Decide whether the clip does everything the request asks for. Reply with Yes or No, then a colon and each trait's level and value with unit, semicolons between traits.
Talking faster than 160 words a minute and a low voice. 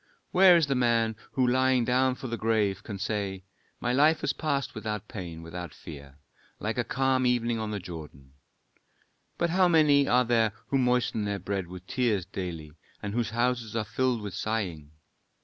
Yes: average, 180 wpm; low, 115 Hz